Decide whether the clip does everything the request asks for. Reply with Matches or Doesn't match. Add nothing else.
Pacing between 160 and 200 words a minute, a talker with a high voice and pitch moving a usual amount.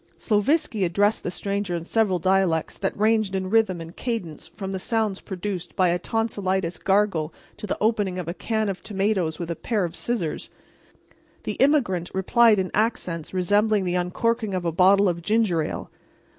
Matches